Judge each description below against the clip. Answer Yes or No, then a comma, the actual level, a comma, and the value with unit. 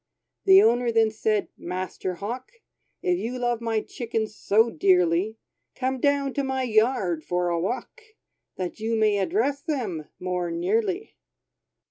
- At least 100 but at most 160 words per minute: Yes, average, 140 wpm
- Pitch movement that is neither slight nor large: No, wide, 5.7 semitones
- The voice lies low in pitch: No, high, 225 Hz